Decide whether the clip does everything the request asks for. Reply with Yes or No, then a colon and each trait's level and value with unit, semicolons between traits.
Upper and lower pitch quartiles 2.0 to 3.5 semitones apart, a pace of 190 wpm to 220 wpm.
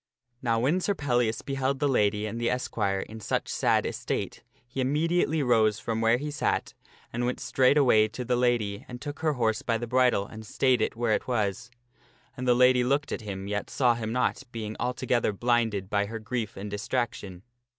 Yes: average, 2.9 semitones; average, 195 wpm